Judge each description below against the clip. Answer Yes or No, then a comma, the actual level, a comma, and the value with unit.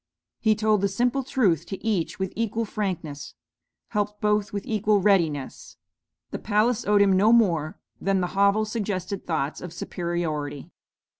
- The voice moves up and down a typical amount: Yes, average, 3.5 semitones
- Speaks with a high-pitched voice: Yes, high, 200 Hz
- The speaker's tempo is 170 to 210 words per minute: No, average, 150 wpm